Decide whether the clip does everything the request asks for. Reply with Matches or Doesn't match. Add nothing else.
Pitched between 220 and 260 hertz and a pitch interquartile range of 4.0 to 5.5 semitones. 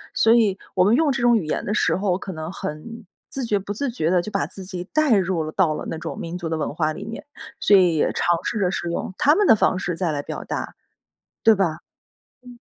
Doesn't match